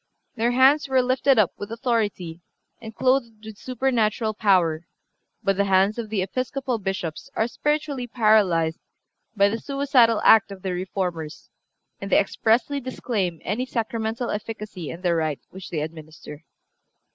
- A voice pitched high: Yes, high, 215 Hz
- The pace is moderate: Yes, average, 150 wpm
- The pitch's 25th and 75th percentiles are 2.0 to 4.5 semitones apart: No, average, 5.0 semitones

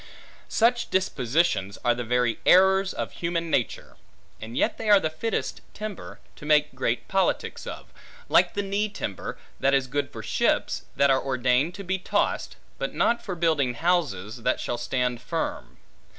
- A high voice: No, medium, 150 Hz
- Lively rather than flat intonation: Yes, wide, 7.4 semitones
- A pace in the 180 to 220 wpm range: No, average, 165 wpm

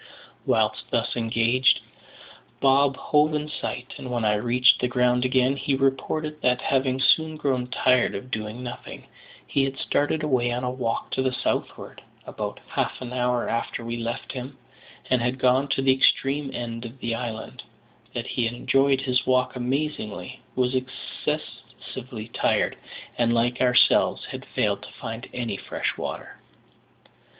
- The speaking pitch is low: Yes, low, 125 Hz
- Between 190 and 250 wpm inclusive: No, average, 160 wpm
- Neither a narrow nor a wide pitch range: No, narrow, 1.9 semitones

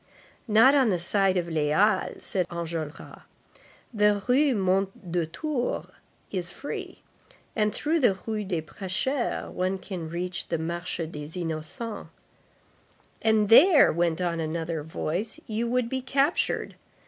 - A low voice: No, high, 190 Hz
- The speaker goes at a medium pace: No, slow, 130 wpm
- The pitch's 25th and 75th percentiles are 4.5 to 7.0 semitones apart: Yes, average, 5.1 semitones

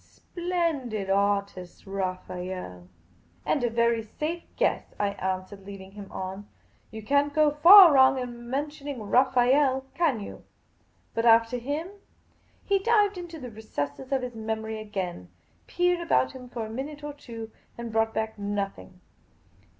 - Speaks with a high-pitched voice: Yes, high, 230 Hz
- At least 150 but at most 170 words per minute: Yes, average, 155 wpm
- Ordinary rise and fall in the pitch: No, wide, 6.2 semitones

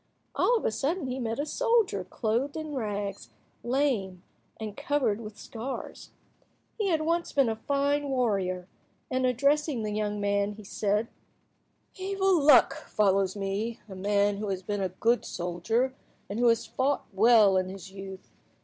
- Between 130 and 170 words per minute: Yes, average, 160 wpm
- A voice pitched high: Yes, high, 225 Hz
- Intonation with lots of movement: Yes, wide, 5.7 semitones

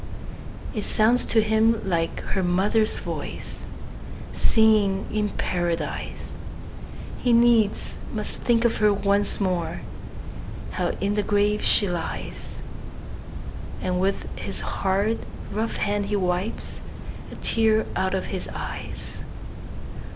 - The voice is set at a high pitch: Yes, high, 205 Hz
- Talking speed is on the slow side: Yes, slow, 115 wpm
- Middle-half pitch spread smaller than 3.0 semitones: Yes, narrow, 2.5 semitones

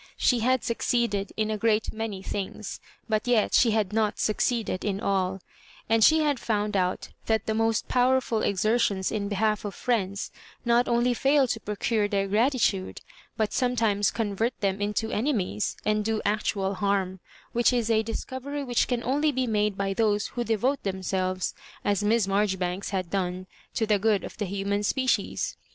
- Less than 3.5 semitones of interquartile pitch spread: Yes, average, 3.0 semitones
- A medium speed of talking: Yes, average, 170 wpm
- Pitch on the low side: No, high, 215 Hz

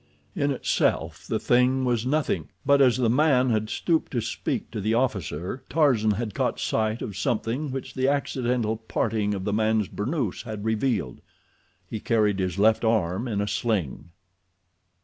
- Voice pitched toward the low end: Yes, low, 110 Hz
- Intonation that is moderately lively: Yes, average, 3.5 semitones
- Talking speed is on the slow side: No, average, 160 wpm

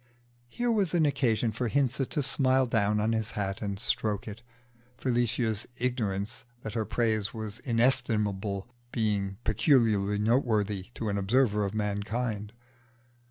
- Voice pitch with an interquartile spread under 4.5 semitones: Yes, average, 3.3 semitones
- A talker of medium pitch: No, low, 110 Hz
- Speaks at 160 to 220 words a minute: No, slow, 135 wpm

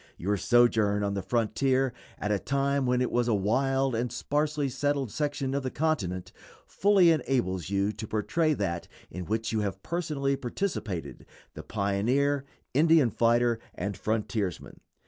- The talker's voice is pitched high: No, low, 120 Hz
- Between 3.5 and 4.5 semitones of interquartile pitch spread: No, wide, 5.4 semitones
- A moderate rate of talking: Yes, average, 150 wpm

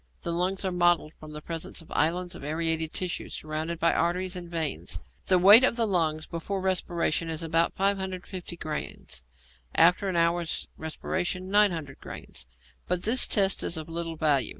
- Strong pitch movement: No, narrow, 2.6 semitones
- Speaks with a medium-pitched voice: Yes, medium, 170 Hz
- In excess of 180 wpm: No, average, 170 wpm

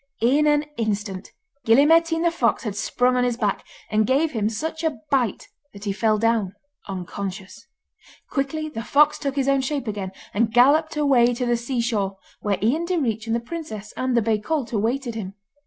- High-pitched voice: Yes, high, 240 Hz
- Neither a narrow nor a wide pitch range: Yes, average, 5.0 semitones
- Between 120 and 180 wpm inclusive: No, average, 190 wpm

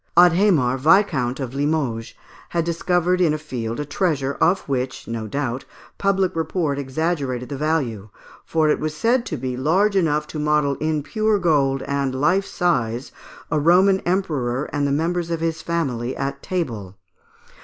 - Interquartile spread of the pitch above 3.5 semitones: Yes, average, 4.7 semitones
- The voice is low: No, medium, 150 Hz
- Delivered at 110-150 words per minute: No, average, 160 wpm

